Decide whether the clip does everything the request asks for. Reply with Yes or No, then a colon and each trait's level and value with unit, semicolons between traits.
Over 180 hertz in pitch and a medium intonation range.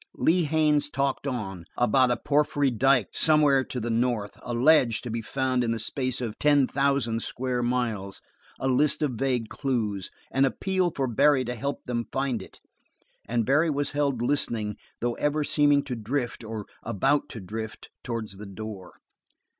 No: low, 125 Hz; average, 3.8 semitones